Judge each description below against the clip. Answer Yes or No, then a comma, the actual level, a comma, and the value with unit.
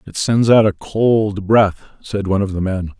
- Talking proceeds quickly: Yes, fast, 220 wpm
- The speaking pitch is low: Yes, low, 100 Hz